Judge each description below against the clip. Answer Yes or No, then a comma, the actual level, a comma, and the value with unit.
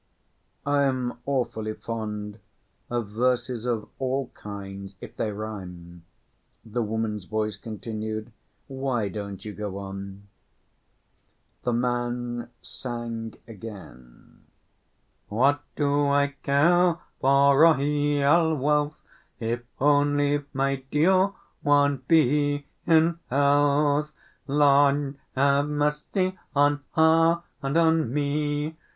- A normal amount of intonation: Yes, average, 4.7 semitones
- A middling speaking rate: No, slow, 100 wpm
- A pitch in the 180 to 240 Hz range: No, low, 135 Hz